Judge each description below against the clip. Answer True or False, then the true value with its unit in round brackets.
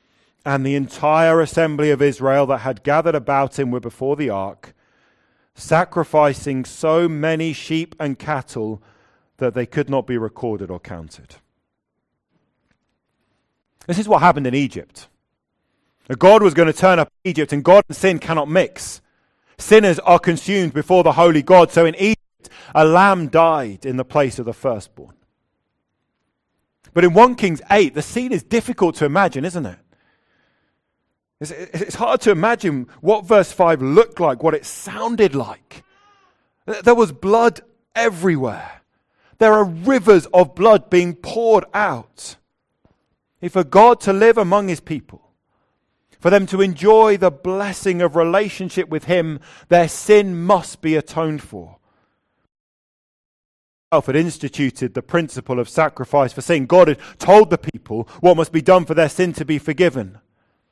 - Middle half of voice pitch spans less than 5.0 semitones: False (5.5 semitones)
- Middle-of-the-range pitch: True (160 Hz)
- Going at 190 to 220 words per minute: False (155 wpm)